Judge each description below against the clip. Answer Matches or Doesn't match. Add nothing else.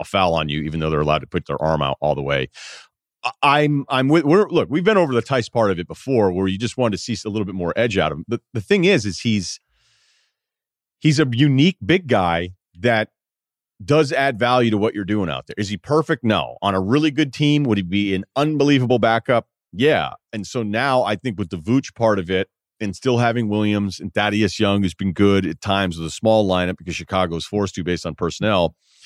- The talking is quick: Matches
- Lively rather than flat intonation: Matches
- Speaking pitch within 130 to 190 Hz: Doesn't match